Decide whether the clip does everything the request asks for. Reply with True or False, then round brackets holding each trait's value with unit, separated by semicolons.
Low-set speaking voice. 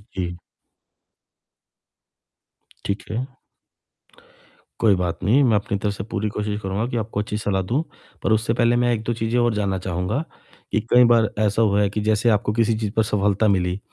True (105 Hz)